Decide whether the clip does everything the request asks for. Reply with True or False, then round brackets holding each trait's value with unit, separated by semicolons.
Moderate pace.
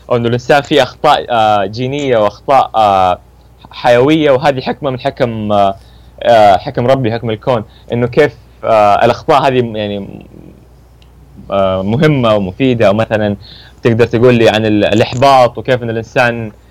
True (110 wpm)